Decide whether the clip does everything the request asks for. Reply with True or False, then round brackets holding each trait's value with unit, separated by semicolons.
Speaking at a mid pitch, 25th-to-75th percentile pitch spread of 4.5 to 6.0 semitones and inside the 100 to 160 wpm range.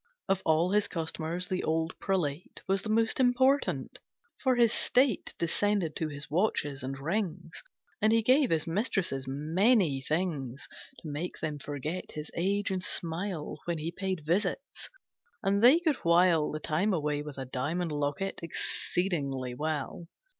True (170 Hz; 4.8 semitones; 155 wpm)